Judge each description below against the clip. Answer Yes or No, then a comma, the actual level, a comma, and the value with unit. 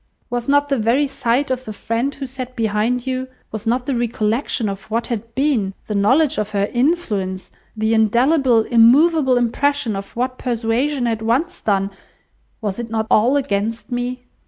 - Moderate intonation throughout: Yes, average, 3.3 semitones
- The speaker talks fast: No, average, 165 wpm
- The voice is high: Yes, high, 240 Hz